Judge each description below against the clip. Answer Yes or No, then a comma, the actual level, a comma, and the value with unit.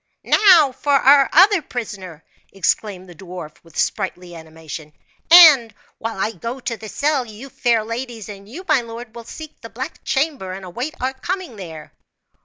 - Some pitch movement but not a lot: No, wide, 6.6 semitones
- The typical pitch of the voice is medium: No, high, 230 Hz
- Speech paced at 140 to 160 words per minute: No, average, 170 wpm